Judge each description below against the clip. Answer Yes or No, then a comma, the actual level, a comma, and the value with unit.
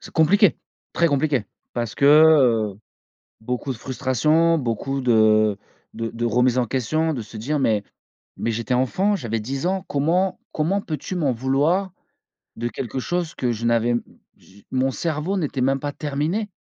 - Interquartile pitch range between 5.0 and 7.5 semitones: Yes, average, 5.3 semitones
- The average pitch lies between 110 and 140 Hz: Yes, low, 135 Hz